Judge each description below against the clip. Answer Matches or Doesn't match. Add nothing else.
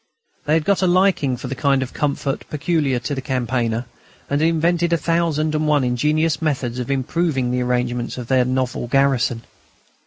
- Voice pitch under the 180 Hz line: Matches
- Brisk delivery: Doesn't match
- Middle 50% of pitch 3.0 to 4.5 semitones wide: Matches